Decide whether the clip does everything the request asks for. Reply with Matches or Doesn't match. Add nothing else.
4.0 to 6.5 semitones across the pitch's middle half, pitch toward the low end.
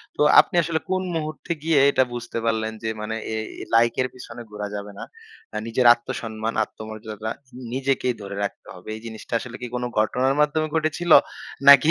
Matches